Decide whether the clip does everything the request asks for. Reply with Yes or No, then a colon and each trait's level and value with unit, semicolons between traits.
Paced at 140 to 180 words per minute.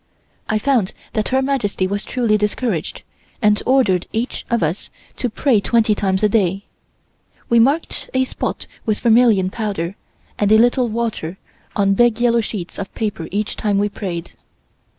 Yes: average, 160 wpm